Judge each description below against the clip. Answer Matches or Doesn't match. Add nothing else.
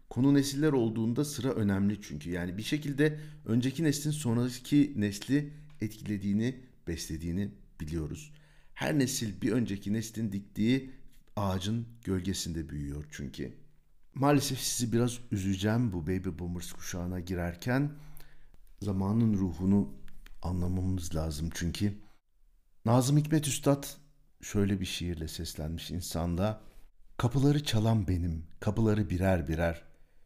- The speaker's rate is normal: Matches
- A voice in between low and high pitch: Doesn't match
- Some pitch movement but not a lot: Doesn't match